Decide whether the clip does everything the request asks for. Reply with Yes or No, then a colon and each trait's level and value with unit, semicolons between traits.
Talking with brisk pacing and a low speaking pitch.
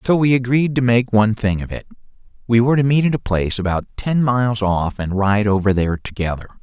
Yes: fast, 225 wpm; low, 110 Hz